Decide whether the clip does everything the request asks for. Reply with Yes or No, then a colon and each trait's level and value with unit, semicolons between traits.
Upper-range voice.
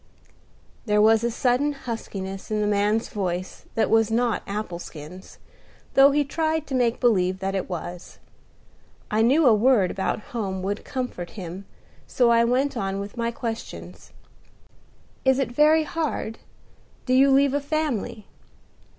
Yes: high, 225 Hz